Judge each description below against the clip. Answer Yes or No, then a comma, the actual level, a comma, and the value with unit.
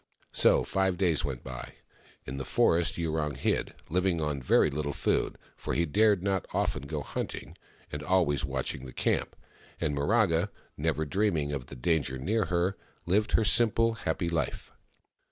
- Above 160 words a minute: Yes, average, 170 wpm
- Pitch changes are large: No, average, 4.9 semitones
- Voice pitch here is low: Yes, very low, 80 Hz